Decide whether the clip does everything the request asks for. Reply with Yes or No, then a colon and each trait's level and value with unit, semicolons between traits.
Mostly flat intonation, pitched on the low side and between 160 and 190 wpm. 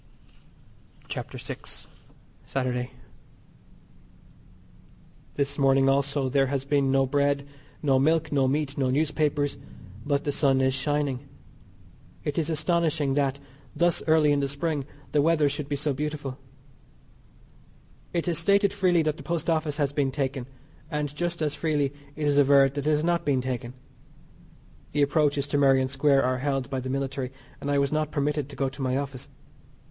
No: narrow, 1.9 semitones; medium, 145 Hz; average, 165 wpm